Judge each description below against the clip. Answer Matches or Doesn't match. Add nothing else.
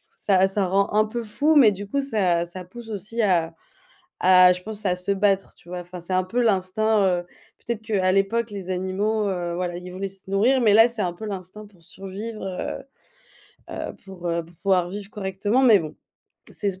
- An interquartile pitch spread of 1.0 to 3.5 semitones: Matches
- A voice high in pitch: Matches